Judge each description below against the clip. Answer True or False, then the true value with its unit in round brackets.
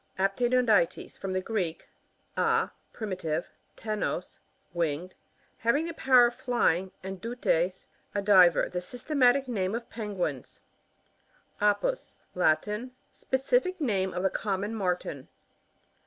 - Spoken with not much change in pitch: False (5.1 semitones)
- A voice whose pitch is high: True (210 Hz)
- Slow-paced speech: True (120 wpm)